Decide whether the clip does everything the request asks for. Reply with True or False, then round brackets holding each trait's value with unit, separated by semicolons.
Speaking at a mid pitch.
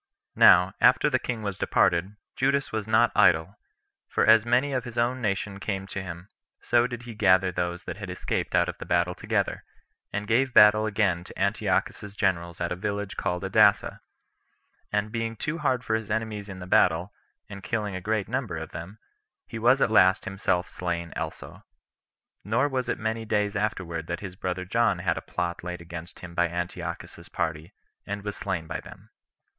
False (100 Hz)